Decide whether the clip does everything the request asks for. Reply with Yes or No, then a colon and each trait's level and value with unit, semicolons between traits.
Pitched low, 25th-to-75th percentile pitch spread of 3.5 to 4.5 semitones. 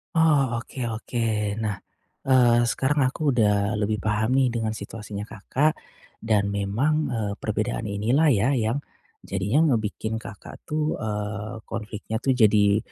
Yes: low, 110 Hz; average, 3.9 semitones